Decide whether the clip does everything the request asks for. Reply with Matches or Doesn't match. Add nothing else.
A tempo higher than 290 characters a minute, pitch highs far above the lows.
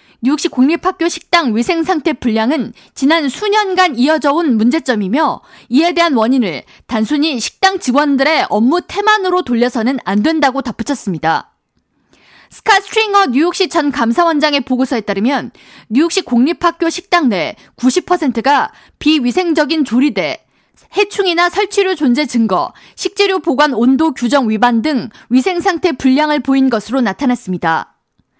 Matches